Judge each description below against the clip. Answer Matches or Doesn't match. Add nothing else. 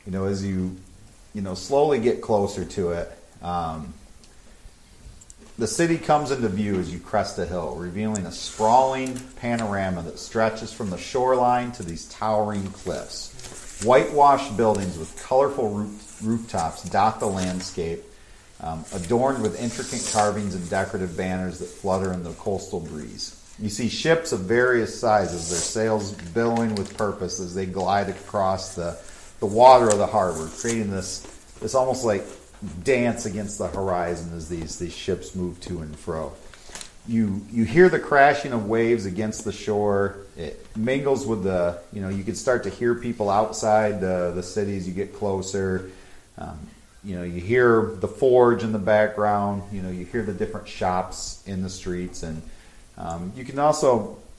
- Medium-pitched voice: Doesn't match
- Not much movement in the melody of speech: Doesn't match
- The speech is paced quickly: Doesn't match